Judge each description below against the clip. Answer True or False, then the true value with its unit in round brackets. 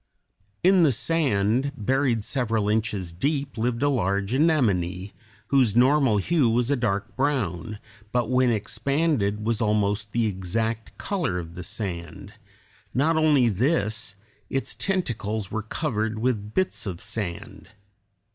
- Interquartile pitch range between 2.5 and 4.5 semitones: False (5.1 semitones)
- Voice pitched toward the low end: True (115 Hz)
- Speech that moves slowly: True (130 wpm)